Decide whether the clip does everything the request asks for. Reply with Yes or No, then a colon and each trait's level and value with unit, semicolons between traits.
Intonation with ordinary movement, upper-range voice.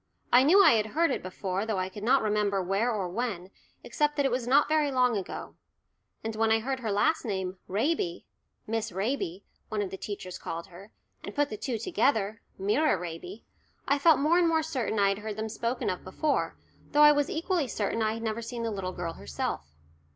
No: wide, 5.8 semitones; high, 220 Hz